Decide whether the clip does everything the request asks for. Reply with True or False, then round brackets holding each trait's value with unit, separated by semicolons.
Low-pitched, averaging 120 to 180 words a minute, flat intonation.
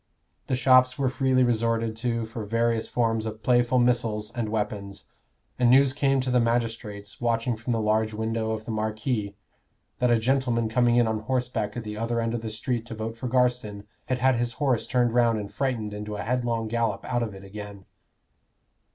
False (115 Hz; 195 wpm; 2.2 semitones)